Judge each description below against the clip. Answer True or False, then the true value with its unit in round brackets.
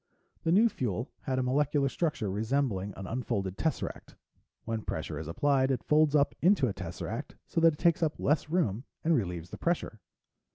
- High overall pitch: False (130 Hz)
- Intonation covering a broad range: True (7.0 semitones)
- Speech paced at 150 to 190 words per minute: True (180 wpm)